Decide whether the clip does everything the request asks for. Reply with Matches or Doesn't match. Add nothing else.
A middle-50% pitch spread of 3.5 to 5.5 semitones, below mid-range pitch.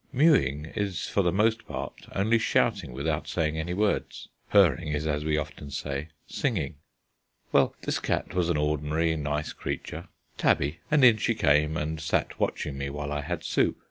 Matches